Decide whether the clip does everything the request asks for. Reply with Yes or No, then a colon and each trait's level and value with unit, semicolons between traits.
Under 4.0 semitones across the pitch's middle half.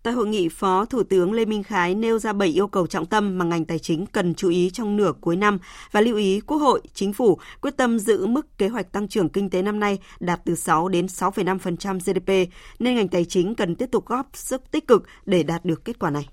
Yes: average, 3.4 semitones